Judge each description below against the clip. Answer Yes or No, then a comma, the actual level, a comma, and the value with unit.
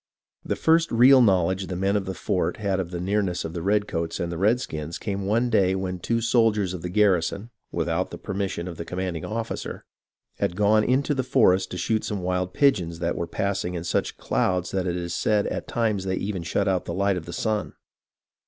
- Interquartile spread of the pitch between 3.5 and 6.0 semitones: No, average, 3.0 semitones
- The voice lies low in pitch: Yes, very low, 95 Hz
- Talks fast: Yes, fast, 220 wpm